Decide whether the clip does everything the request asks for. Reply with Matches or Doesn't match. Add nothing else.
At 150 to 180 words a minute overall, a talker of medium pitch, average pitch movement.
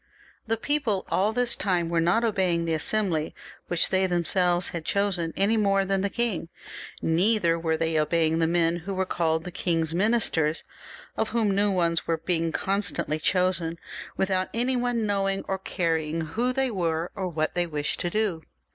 Matches